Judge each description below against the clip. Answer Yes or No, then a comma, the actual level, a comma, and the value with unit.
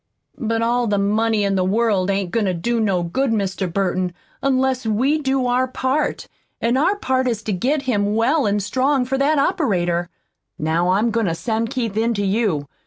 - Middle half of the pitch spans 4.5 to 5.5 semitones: Yes, average, 4.8 semitones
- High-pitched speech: Yes, high, 225 Hz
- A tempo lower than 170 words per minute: No, average, 195 wpm